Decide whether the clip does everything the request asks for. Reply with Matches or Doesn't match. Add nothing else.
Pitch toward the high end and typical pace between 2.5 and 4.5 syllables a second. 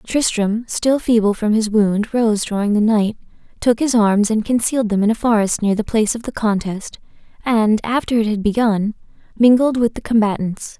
Doesn't match